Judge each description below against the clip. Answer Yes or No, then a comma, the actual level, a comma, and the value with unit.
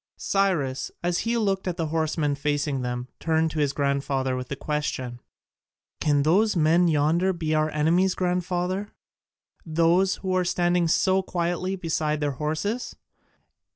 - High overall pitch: No, medium, 160 Hz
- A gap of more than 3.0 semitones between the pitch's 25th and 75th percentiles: Yes, average, 3.6 semitones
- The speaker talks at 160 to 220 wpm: No, average, 145 wpm